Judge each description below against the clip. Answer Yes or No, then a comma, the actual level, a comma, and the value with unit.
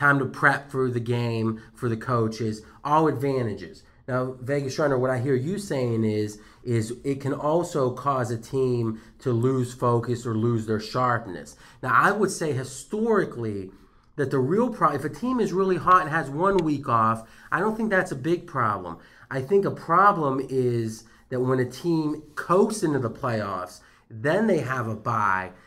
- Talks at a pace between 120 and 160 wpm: No, average, 185 wpm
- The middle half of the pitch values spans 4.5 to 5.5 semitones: Yes, average, 5.0 semitones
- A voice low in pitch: Yes, low, 130 Hz